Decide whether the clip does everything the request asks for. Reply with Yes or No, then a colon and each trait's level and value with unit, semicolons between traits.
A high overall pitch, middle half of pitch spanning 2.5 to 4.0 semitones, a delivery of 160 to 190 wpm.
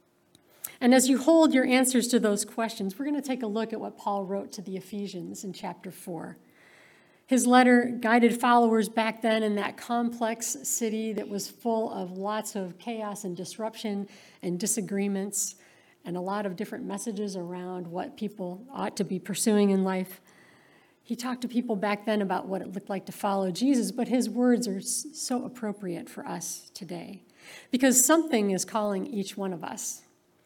Yes: high, 215 Hz; average, 3.4 semitones; average, 180 wpm